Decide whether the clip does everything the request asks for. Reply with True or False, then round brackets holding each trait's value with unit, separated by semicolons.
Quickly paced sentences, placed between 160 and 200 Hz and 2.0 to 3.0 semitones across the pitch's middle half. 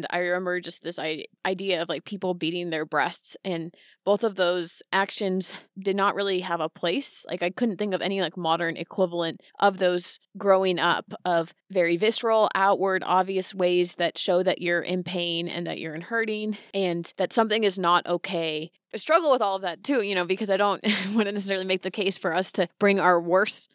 True (210 wpm; 185 Hz; 2.4 semitones)